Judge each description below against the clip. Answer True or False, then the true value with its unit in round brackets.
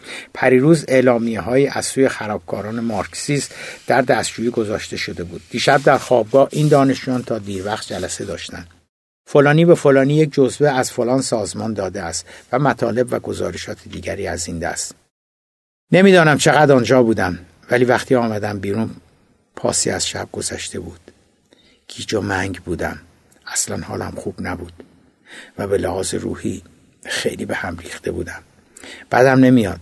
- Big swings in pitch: False (4.3 semitones)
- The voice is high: False (125 Hz)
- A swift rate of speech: False (145 wpm)